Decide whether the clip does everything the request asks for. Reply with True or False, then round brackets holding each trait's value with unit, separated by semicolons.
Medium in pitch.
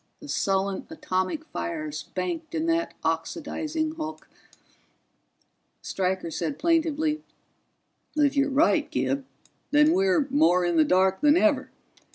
False (295 Hz)